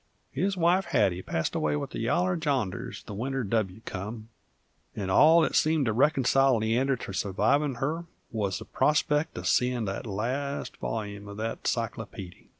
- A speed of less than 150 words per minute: No, average, 160 wpm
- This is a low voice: Yes, low, 120 Hz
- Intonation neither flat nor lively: No, wide, 6.0 semitones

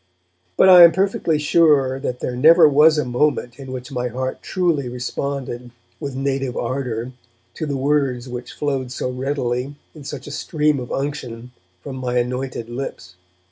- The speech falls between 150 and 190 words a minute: Yes, average, 165 wpm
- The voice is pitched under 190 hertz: Yes, low, 135 Hz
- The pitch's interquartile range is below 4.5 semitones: Yes, average, 3.0 semitones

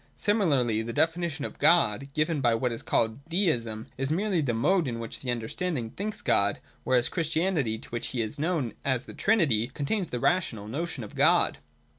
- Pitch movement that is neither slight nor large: No, wide, 6.7 semitones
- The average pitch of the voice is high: No, medium, 140 Hz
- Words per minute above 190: No, average, 185 wpm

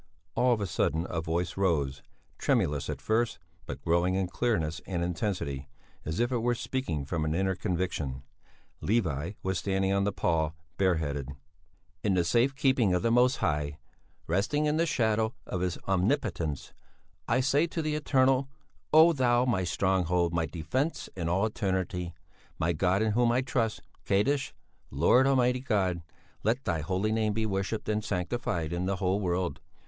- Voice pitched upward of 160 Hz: No, very low, 95 Hz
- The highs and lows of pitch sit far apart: Yes, wide, 5.8 semitones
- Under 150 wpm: No, average, 170 wpm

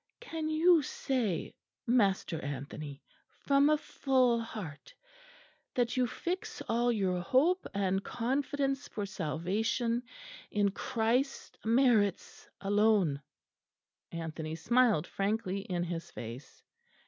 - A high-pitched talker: Yes, high, 220 Hz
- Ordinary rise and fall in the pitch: No, wide, 6.2 semitones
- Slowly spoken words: Yes, slow, 100 wpm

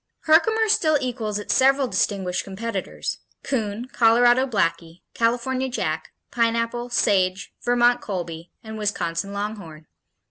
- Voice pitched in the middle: No, high, 230 Hz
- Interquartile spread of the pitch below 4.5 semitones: Yes, average, 3.9 semitones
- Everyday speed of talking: No, slow, 110 wpm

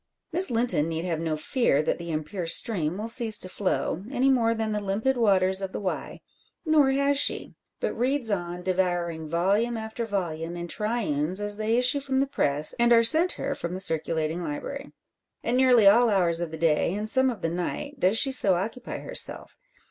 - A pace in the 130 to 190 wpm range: No, average, 200 wpm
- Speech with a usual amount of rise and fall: No, wide, 5.9 semitones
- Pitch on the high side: Yes, high, 205 Hz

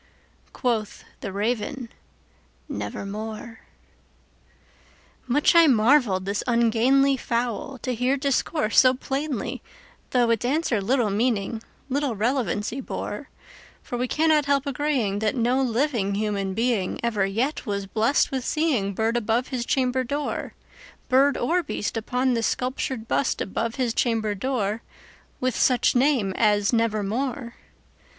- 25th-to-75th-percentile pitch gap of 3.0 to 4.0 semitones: Yes, average, 3.7 semitones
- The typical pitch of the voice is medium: No, high, 240 Hz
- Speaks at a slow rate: Yes, slow, 115 wpm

